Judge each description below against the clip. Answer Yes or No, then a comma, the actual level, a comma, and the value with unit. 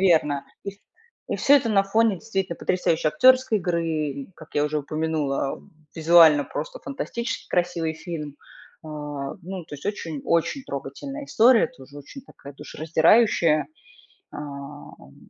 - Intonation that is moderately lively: No, wide, 5.9 semitones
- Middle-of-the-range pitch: Yes, medium, 165 Hz